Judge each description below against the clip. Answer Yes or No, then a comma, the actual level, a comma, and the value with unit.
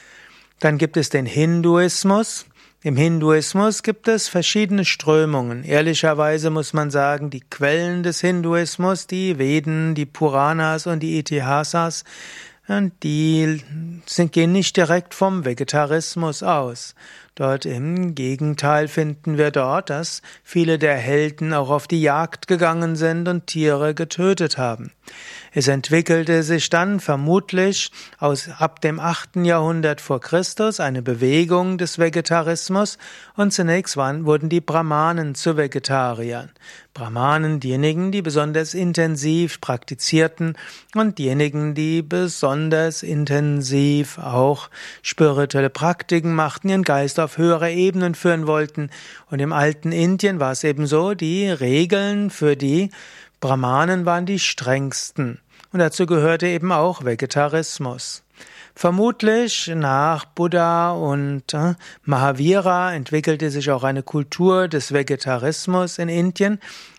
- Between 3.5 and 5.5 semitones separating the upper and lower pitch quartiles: No, average, 3.1 semitones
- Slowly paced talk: Yes, slow, 120 wpm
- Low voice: No, medium, 160 Hz